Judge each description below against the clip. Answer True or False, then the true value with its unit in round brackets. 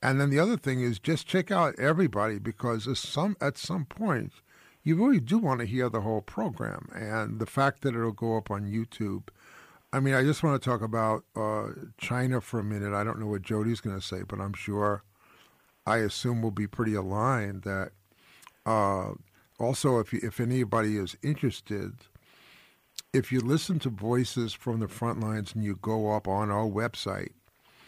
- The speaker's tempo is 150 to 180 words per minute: False (190 wpm)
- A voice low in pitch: True (115 Hz)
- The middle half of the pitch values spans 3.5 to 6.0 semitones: True (3.9 semitones)